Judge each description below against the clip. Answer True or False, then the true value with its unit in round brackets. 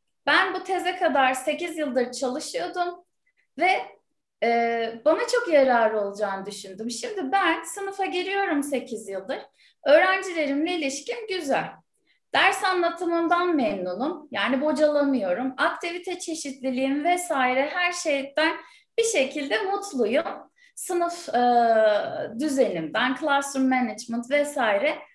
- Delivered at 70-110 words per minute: True (95 wpm)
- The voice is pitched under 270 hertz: False (300 Hz)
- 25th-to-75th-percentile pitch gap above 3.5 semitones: True (5.5 semitones)